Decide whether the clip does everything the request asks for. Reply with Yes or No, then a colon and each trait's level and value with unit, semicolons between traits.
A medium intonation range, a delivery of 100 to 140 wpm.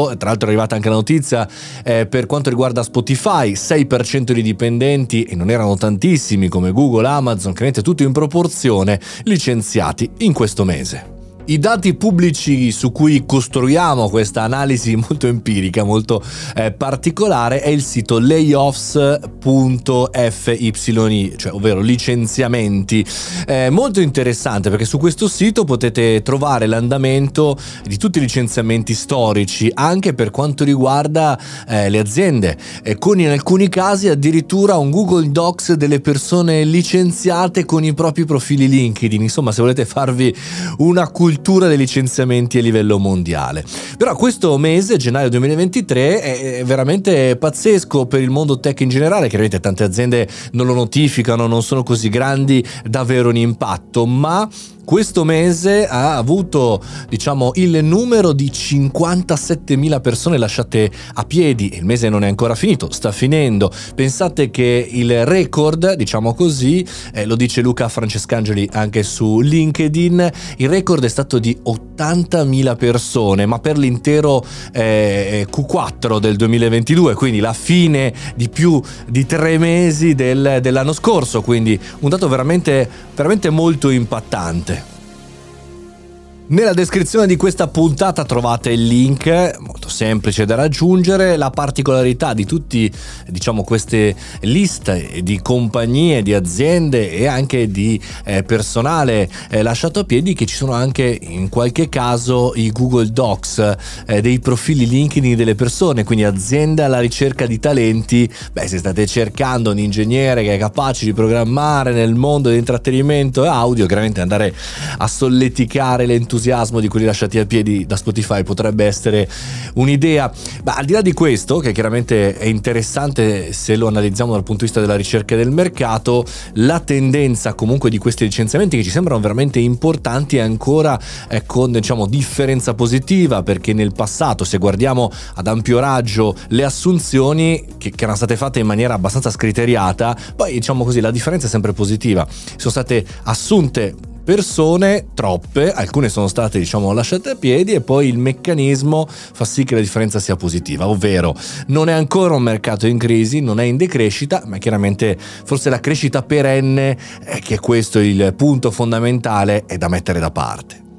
No: average, 5.0 semitones; average, 150 wpm